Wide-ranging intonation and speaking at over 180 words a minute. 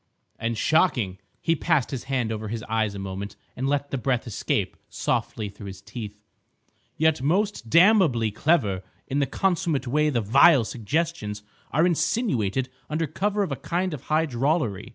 No: wide, 6.9 semitones; average, 165 wpm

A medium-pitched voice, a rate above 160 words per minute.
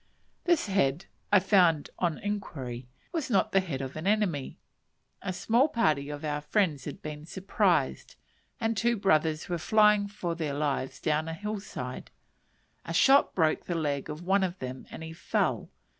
Yes: medium, 170 Hz; average, 175 wpm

